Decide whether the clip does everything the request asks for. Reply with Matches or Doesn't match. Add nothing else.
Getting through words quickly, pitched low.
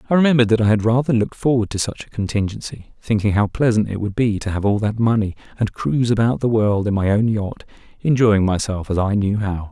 Matches